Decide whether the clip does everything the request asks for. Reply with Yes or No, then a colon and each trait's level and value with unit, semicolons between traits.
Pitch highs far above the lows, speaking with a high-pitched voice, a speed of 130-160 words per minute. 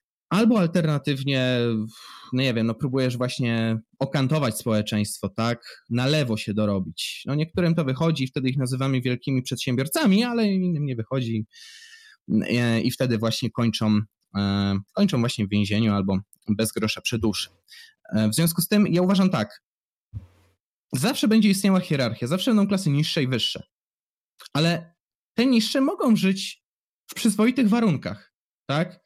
No: wide, 8.7 semitones; low, 135 Hz; average, 145 wpm